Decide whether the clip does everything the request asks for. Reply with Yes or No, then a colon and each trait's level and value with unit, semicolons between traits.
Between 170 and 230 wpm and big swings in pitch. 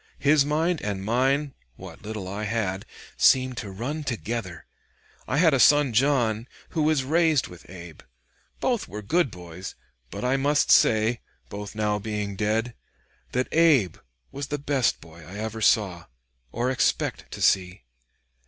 No: average, 155 wpm; wide, 5.8 semitones